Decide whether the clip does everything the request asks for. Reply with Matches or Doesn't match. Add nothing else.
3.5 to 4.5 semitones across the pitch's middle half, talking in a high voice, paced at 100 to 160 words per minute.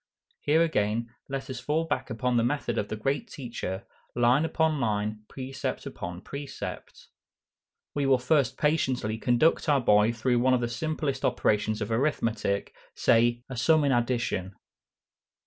Doesn't match